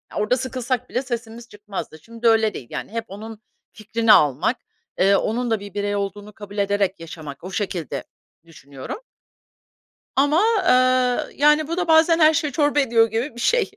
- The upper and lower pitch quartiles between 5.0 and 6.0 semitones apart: No, average, 4.2 semitones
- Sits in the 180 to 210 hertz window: No, high, 225 Hz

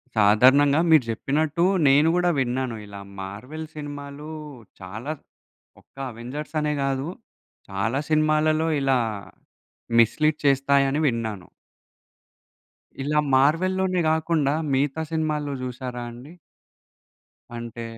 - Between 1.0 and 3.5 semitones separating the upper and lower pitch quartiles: No, average, 3.9 semitones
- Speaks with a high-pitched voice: No, medium, 140 Hz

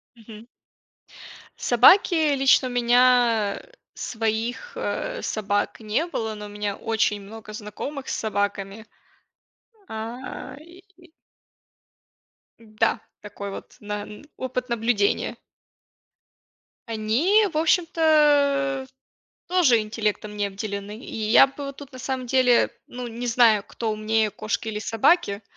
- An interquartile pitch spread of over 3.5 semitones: Yes, average, 4.1 semitones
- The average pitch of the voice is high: Yes, high, 230 Hz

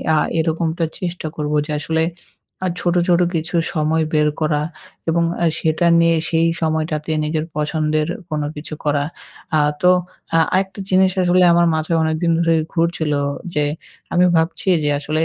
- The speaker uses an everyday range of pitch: No, narrow, 1.9 semitones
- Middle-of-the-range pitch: Yes, medium, 160 Hz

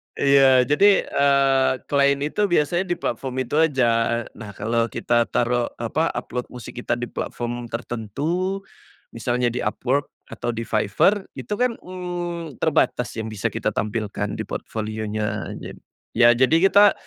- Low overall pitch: Yes, low, 130 Hz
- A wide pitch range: Yes, wide, 5.7 semitones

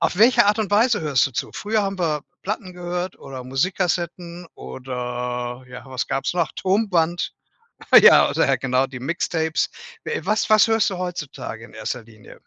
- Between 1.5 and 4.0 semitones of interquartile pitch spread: No, wide, 6.9 semitones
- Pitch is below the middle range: No, medium, 170 Hz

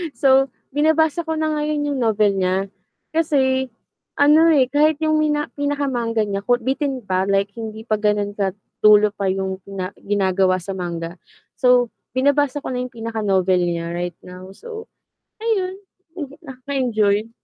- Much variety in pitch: Yes, wide, 6.6 semitones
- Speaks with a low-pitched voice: No, high, 240 Hz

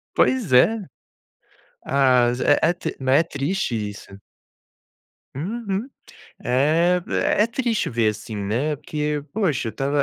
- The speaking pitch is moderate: Yes, medium, 145 Hz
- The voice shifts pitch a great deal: Yes, wide, 7.0 semitones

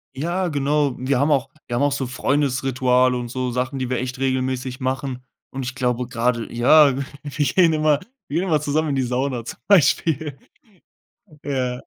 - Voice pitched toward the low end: Yes, low, 130 Hz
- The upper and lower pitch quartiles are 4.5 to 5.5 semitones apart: No, narrow, 2.4 semitones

